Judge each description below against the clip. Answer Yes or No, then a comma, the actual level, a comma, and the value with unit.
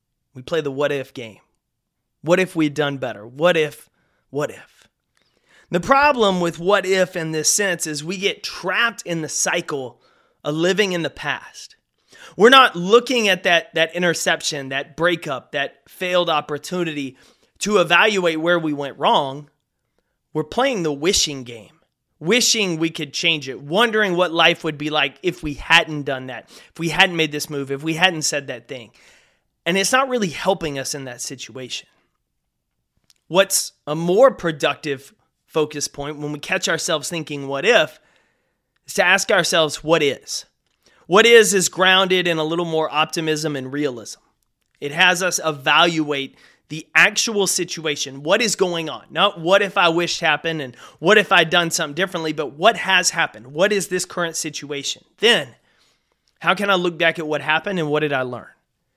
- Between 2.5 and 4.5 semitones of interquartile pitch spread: Yes, average, 3.8 semitones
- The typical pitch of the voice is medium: Yes, medium, 165 Hz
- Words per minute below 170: No, average, 175 wpm